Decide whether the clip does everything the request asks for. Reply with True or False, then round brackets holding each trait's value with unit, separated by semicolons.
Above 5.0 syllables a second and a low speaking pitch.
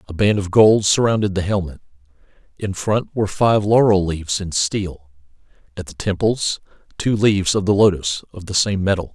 True (5.2 syllables/s; 95 Hz)